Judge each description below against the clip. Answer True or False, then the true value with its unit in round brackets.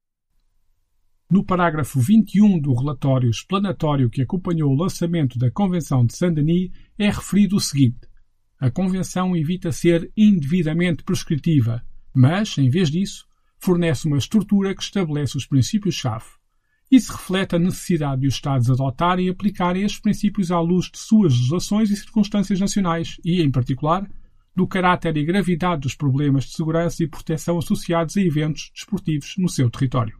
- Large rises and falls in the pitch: True (5.7 semitones)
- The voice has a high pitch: False (170 Hz)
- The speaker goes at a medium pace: True (150 wpm)